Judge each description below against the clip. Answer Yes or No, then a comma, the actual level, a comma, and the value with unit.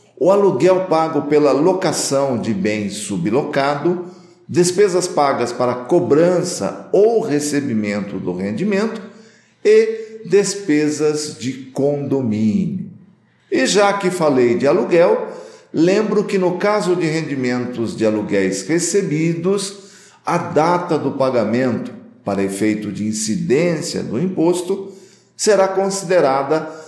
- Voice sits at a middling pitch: Yes, medium, 170 Hz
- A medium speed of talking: No, slow, 105 wpm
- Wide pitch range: Yes, wide, 6.5 semitones